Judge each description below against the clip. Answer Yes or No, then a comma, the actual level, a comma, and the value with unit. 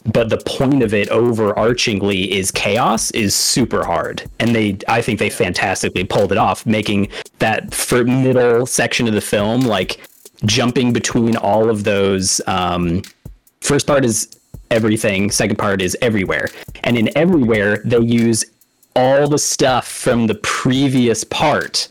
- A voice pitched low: Yes, low, 110 Hz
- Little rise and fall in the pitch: No, average, 3.1 semitones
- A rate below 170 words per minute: Yes, average, 150 wpm